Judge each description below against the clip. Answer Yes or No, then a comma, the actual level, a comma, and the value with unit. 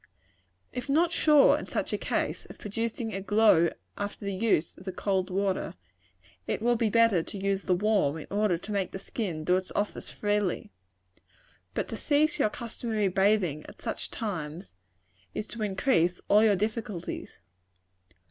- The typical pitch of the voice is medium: No, high, 205 Hz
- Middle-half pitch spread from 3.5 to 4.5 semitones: No, average, 3.1 semitones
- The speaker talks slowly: No, average, 165 wpm